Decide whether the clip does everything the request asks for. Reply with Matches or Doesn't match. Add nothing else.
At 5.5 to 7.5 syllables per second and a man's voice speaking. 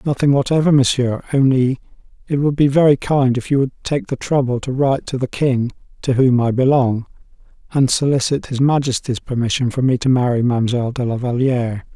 Matches